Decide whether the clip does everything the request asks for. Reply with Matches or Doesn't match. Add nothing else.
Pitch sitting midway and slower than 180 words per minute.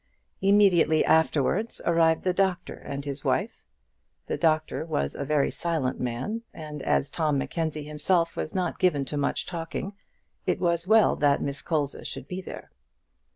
Matches